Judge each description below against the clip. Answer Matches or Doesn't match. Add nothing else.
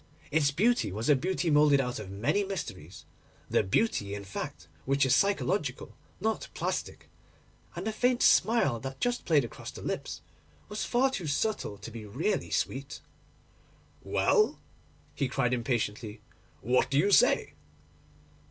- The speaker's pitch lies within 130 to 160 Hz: Matches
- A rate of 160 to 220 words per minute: Doesn't match